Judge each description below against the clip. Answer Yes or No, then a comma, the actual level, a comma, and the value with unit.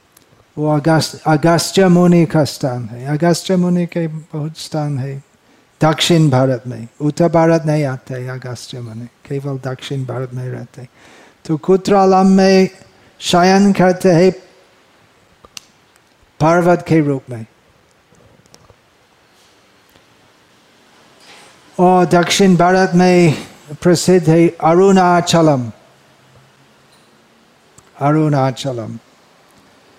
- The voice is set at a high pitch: No, medium, 155 Hz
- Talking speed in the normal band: No, slow, 95 wpm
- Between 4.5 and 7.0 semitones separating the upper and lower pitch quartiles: Yes, average, 5.1 semitones